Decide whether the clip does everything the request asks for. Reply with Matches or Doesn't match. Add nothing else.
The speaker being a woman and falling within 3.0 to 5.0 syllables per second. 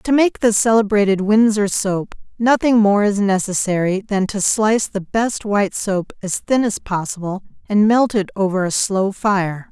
Matches